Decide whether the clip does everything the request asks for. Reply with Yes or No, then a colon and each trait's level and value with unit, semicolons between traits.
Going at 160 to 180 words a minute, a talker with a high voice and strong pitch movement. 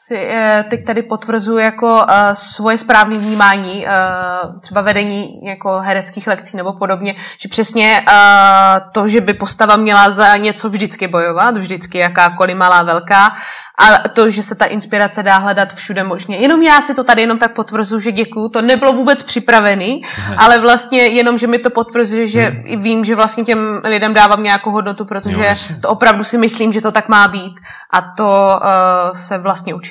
No: fast, 170 wpm; high, 210 Hz; narrow, 2.6 semitones